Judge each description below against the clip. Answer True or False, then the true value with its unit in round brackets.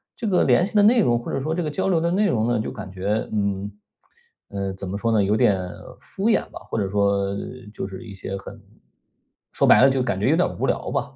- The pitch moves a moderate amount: False (8.8 semitones)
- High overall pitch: False (110 Hz)